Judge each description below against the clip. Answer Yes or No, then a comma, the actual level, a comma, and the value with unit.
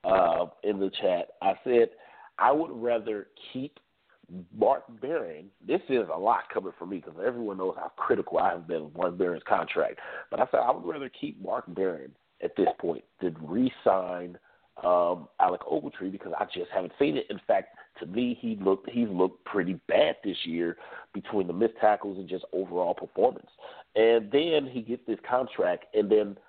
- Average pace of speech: Yes, average, 185 wpm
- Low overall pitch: Yes, low, 115 Hz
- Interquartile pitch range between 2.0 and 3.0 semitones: No, average, 5.3 semitones